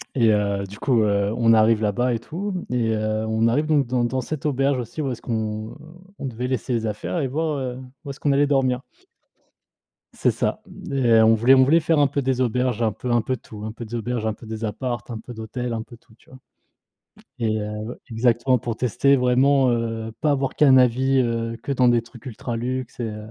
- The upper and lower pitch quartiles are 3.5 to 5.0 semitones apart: No, average, 2.9 semitones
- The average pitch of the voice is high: No, low, 120 Hz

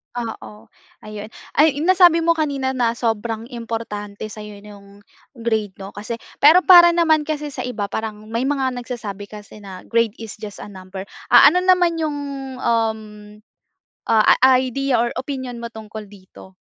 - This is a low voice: No, high, 230 Hz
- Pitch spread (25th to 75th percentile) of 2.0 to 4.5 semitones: No, average, 5.0 semitones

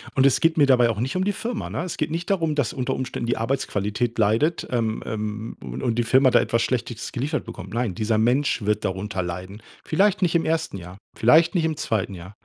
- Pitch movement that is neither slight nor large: No, wide, 6.4 semitones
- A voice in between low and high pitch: No, low, 120 Hz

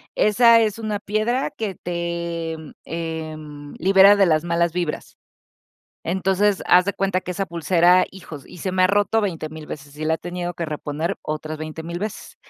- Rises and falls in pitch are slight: No, average, 3.5 semitones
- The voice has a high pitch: No, medium, 175 Hz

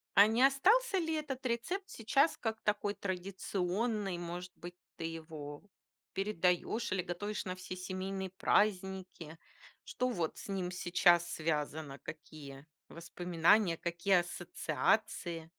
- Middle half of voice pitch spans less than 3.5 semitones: No, average, 4.1 semitones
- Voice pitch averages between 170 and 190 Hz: Yes, medium, 185 Hz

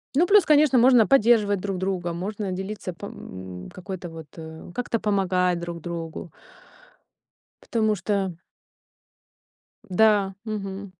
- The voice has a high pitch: Yes, high, 195 Hz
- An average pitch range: Yes, average, 3.7 semitones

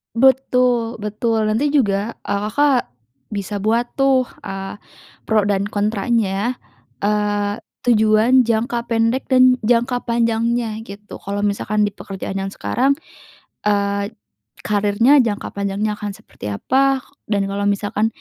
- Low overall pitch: No, high, 215 Hz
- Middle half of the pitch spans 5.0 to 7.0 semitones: No, average, 3.0 semitones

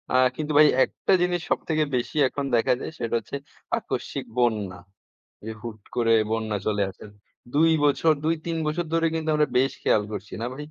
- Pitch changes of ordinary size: No, wide, 6.1 semitones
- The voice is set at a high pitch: No, low, 135 Hz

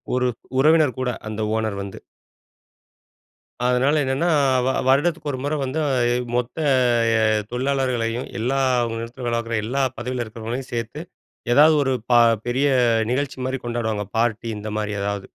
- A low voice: Yes, low, 125 Hz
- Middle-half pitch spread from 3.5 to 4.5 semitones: No, average, 2.9 semitones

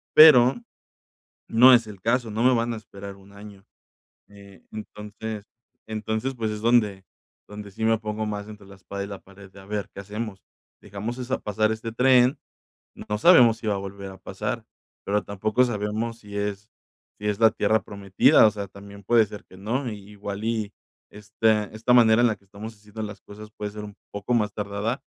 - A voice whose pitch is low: Yes, low, 105 Hz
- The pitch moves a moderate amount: No, narrow, 2.0 semitones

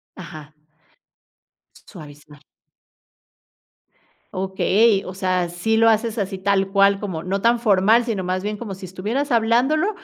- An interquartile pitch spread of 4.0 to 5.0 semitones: No, average, 3.4 semitones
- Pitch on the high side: Yes, high, 195 Hz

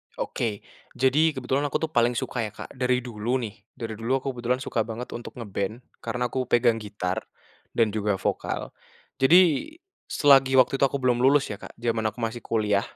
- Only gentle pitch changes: No, average, 3.0 semitones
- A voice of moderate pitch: No, low, 120 Hz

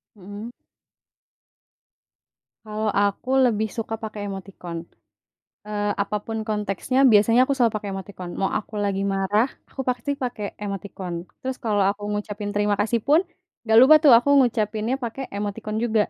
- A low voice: No, high, 210 Hz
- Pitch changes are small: Yes, narrow, 2.3 semitones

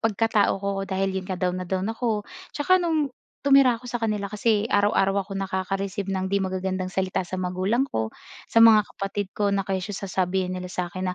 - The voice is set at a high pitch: Yes, high, 195 Hz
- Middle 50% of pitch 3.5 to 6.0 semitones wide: No, average, 2.7 semitones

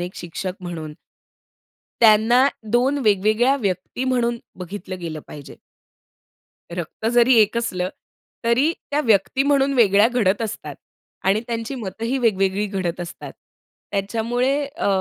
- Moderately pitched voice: No, high, 220 Hz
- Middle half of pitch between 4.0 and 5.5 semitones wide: Yes, average, 4.6 semitones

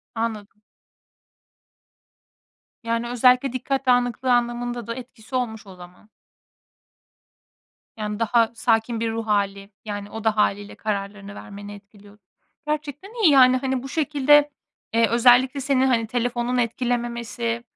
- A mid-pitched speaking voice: No, high, 235 Hz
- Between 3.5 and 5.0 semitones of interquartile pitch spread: No, average, 3.1 semitones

